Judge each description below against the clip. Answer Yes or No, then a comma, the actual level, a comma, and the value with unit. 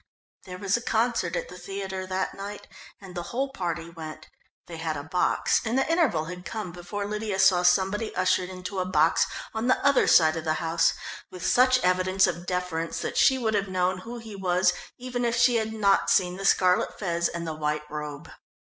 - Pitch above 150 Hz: Yes, medium, 185 Hz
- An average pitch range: Yes, average, 3.7 semitones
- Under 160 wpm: No, fast, 205 wpm